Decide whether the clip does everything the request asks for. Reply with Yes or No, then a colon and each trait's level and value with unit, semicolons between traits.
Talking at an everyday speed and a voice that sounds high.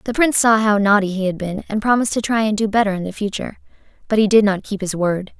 No: fast, 265 wpm; high, 210 Hz